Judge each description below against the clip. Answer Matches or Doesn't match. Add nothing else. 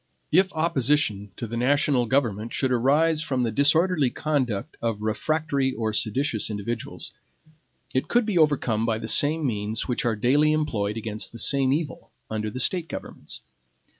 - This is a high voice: Doesn't match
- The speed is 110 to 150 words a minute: Doesn't match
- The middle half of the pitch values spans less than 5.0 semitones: Doesn't match